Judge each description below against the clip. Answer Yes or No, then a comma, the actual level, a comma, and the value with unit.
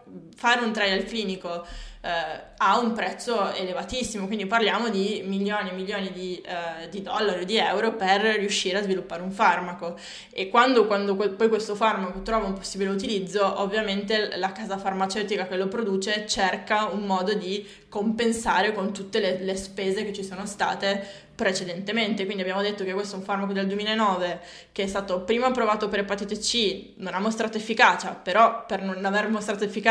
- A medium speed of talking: No, fast, 180 wpm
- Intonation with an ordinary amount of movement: No, narrow, 2.1 semitones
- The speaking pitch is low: No, high, 200 Hz